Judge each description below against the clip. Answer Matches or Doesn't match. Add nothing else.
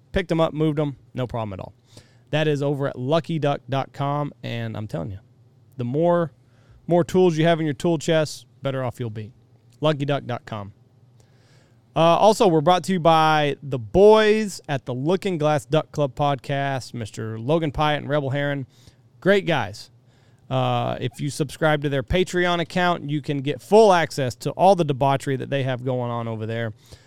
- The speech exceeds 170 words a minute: Matches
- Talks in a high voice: Doesn't match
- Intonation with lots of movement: Doesn't match